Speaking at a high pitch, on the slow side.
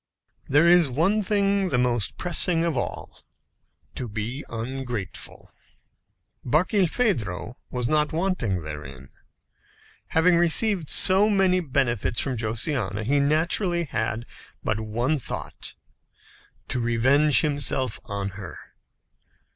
No: medium, 140 Hz; slow, 105 wpm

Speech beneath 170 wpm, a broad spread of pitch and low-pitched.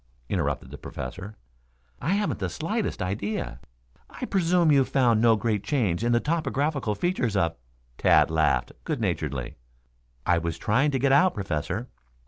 Yes: average, 155 wpm; wide, 8.5 semitones; low, 115 Hz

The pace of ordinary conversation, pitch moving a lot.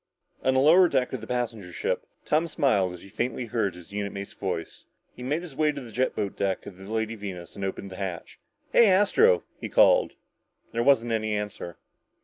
No: fast, 210 wpm; wide, 6.0 semitones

